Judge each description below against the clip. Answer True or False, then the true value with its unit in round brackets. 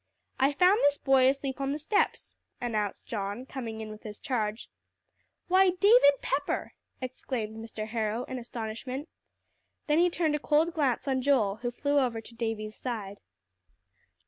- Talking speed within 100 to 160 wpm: True (155 wpm)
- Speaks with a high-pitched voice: True (255 Hz)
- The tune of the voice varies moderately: True (4.5 semitones)